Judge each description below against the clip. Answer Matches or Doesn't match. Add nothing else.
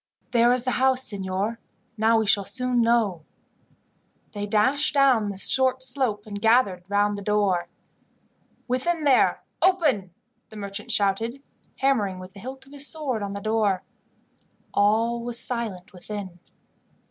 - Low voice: Doesn't match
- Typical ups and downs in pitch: Matches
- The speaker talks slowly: Doesn't match